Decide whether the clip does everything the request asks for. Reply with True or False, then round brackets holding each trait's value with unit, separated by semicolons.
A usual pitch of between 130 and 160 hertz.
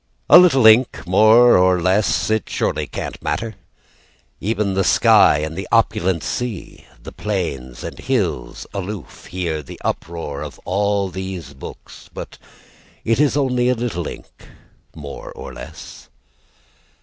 False (95 Hz)